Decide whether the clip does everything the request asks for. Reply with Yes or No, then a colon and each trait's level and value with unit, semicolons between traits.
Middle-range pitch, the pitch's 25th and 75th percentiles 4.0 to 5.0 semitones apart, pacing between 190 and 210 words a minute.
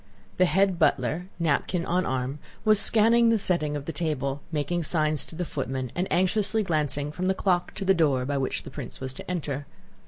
Yes: medium, 165 Hz; average, 4.5 semitones; average, 200 wpm